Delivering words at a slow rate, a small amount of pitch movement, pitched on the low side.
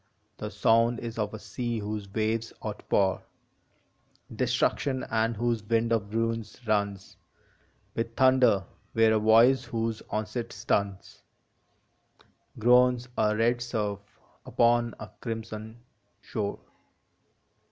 Yes: slow, 110 wpm; narrow, 1.7 semitones; low, 115 Hz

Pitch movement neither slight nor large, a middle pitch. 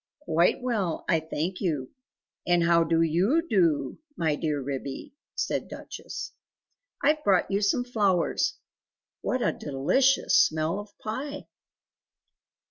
No: wide, 5.8 semitones; medium, 175 Hz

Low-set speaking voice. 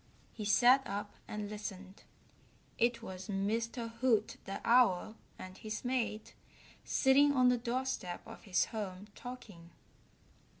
No: high, 215 Hz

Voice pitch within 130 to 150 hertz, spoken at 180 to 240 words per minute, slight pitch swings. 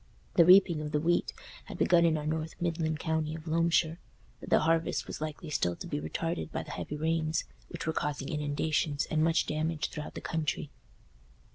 No: medium, 160 Hz; average, 190 wpm; narrow, 1.5 semitones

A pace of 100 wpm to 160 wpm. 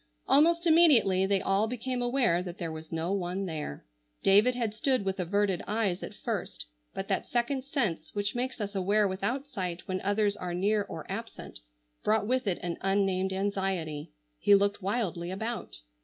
No: average, 170 wpm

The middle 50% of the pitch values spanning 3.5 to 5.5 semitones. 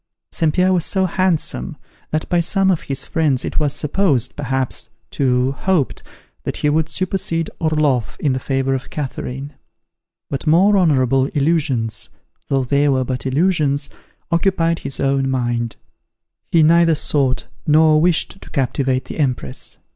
Yes: average, 3.9 semitones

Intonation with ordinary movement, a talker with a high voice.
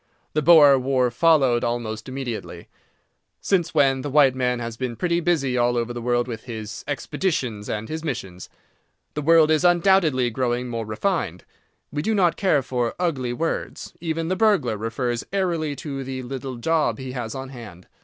No: average, 5.0 semitones; low, 130 Hz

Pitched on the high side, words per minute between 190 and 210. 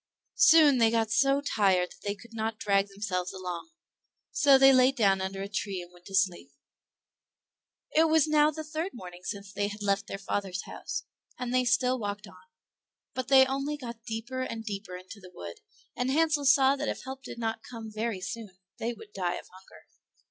Yes: high, 225 Hz; average, 200 wpm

